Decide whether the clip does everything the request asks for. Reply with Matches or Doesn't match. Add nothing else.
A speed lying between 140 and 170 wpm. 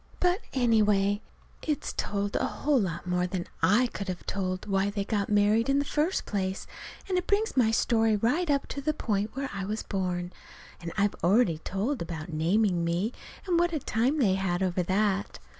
Doesn't match